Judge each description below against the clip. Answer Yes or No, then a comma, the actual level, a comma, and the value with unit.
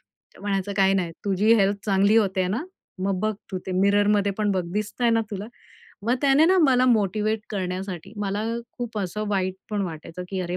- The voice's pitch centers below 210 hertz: Yes, high, 200 Hz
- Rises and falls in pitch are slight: Yes, narrow, 2.1 semitones